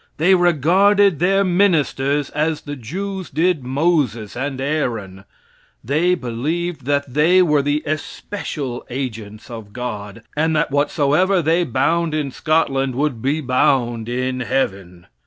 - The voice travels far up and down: No, average, 4.9 semitones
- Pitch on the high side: No, medium, 145 Hz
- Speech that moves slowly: Yes, slow, 130 wpm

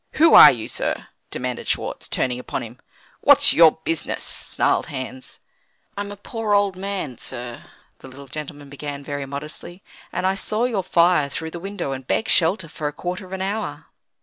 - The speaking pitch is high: No, medium, 160 Hz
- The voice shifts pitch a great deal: Yes, wide, 5.8 semitones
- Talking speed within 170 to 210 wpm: Yes, average, 180 wpm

